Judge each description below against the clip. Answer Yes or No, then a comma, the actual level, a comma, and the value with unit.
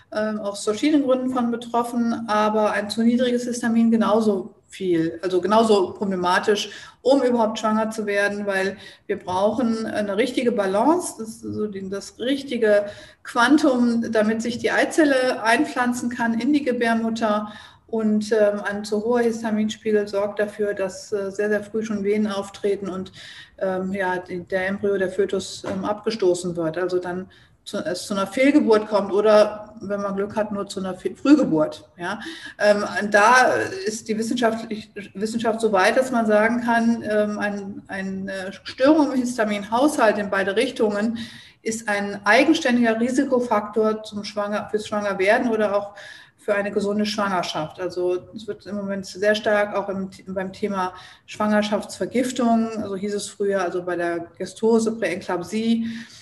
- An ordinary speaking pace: Yes, average, 145 wpm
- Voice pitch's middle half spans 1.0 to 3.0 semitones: Yes, narrow, 2.6 semitones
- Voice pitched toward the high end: Yes, high, 210 Hz